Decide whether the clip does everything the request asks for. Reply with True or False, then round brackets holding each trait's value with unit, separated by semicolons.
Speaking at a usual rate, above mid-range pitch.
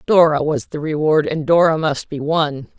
False (195 wpm; 155 Hz)